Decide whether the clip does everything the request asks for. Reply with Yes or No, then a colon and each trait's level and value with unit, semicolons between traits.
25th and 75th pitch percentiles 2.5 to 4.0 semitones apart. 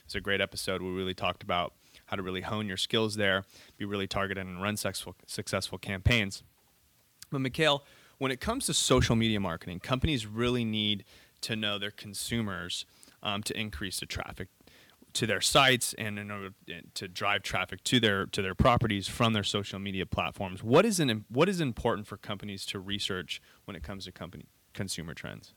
Yes: average, 2.9 semitones